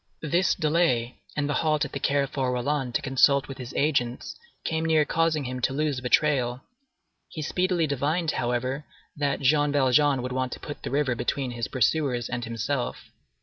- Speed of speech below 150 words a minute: No, average, 180 wpm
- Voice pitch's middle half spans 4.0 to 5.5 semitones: No, average, 3.2 semitones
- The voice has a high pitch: No, medium, 140 Hz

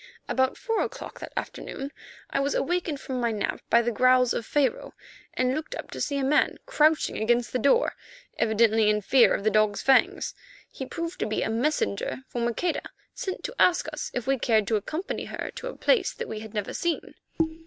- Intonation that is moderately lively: No, wide, 5.9 semitones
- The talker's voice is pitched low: No, very high, 260 Hz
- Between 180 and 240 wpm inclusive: Yes, fast, 205 wpm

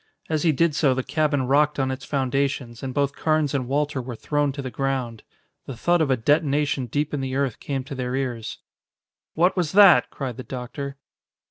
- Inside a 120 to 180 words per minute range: No, fast, 205 wpm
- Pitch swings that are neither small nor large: No, narrow, 2.3 semitones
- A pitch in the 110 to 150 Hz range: Yes, medium, 140 Hz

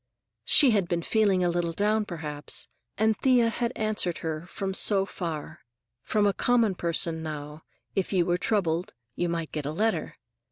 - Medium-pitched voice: Yes, medium, 180 Hz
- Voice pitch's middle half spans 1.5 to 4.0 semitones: No, average, 4.5 semitones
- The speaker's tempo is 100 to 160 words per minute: No, average, 170 wpm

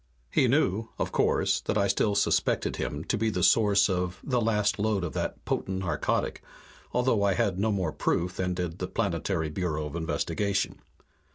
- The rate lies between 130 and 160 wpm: No, average, 180 wpm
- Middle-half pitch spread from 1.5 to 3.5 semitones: Yes, average, 2.9 semitones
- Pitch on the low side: Yes, very low, 95 Hz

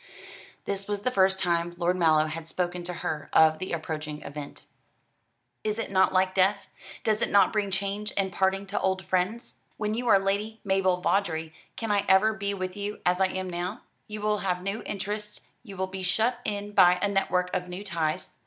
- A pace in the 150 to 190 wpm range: No, average, 200 wpm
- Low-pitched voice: No, high, 190 Hz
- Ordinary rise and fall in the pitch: No, narrow, 2.3 semitones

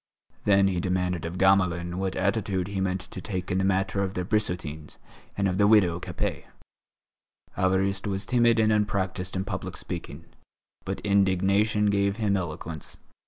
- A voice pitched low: Yes, very low, 95 Hz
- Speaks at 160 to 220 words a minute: Yes, average, 165 wpm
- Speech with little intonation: Yes, narrow, 1.8 semitones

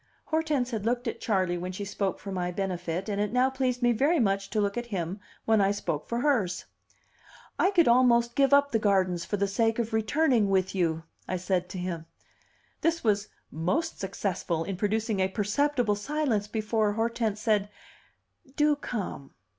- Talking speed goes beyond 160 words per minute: Yes, average, 180 wpm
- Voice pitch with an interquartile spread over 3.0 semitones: Yes, average, 4.2 semitones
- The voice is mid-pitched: No, high, 210 Hz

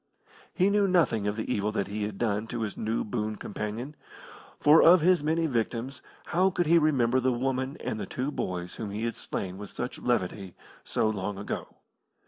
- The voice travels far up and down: Yes, wide, 6.1 semitones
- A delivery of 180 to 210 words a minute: Yes, average, 195 wpm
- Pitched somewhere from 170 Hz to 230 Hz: No, low, 115 Hz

